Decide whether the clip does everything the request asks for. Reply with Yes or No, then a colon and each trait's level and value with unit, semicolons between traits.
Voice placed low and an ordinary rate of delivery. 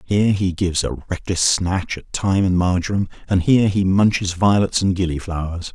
Yes: very low, 95 Hz; average, 175 wpm